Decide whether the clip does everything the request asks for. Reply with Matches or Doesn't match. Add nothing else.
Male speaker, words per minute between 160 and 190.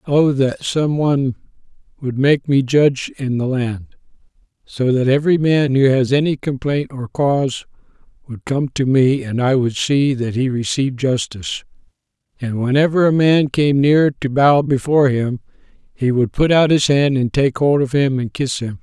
Matches